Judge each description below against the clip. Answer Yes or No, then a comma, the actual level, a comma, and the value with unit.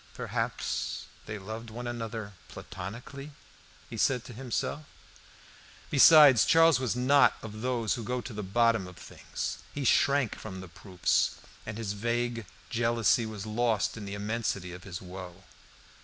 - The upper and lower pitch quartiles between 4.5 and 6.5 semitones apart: No, average, 3.3 semitones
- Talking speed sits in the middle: Yes, average, 150 wpm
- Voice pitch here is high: No, low, 115 Hz